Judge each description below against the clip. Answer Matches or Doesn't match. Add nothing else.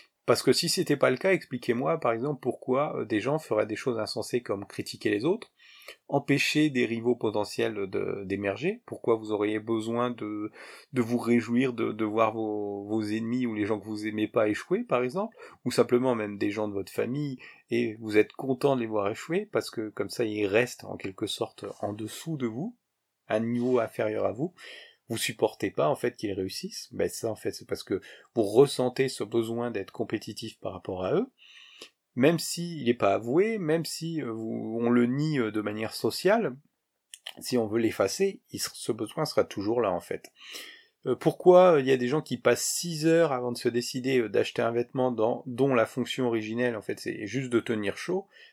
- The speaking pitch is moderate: Doesn't match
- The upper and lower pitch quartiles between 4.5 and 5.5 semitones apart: Matches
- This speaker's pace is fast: Doesn't match